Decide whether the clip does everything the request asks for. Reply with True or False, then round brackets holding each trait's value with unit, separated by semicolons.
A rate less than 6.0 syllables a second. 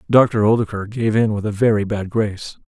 True (5.4 syllables/s)